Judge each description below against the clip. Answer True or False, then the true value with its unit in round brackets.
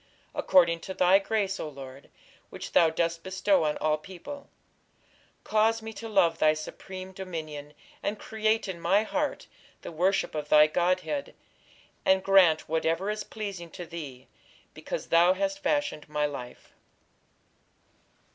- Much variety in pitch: False (4.7 semitones)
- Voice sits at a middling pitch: True (180 Hz)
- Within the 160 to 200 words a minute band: False (140 wpm)